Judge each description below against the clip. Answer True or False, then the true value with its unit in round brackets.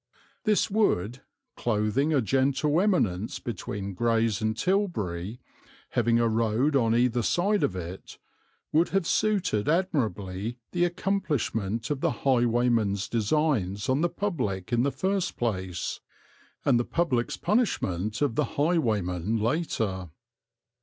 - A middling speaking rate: False (125 wpm)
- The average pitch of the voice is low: True (120 Hz)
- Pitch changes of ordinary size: False (7.2 semitones)